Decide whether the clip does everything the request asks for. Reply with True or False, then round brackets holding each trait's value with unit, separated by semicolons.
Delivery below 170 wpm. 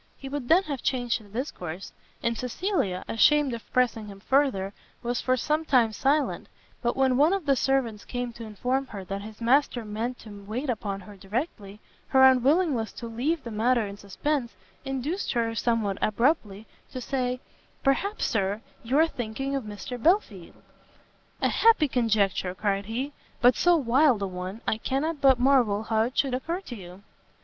False (175 wpm)